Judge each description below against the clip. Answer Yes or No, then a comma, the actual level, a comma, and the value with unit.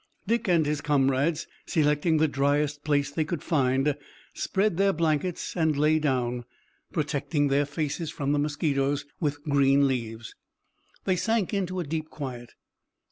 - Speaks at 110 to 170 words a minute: Yes, average, 145 wpm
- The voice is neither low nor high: Yes, medium, 150 Hz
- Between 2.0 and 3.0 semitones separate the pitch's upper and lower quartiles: Yes, average, 2.7 semitones